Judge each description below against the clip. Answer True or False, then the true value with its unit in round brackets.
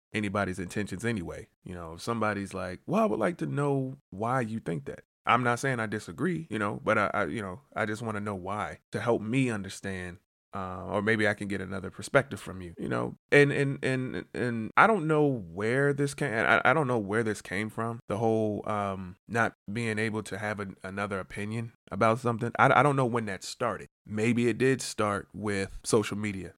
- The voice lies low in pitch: True (105 Hz)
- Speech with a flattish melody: False (3.5 semitones)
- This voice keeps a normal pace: False (220 wpm)